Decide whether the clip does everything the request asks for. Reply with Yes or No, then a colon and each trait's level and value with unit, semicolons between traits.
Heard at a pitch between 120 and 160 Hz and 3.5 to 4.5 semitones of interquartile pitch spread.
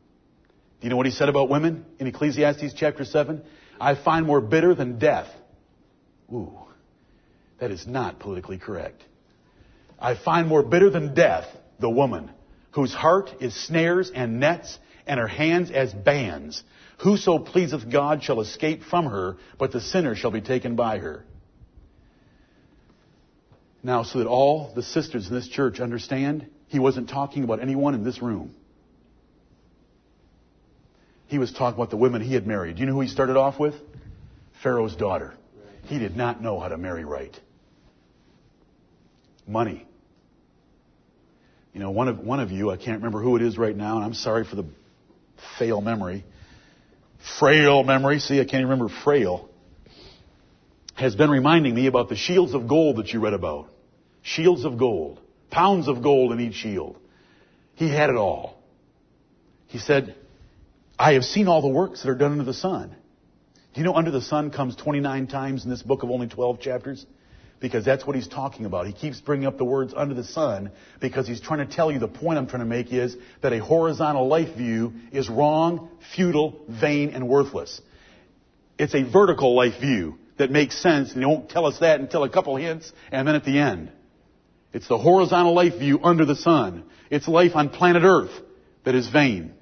Yes: low, 135 Hz; average, 3.9 semitones